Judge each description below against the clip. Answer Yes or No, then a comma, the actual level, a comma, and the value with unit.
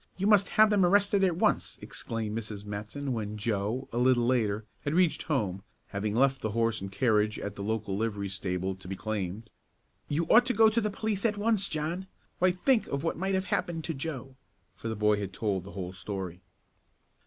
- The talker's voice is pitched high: No, low, 115 Hz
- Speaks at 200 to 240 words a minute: Yes, fast, 205 wpm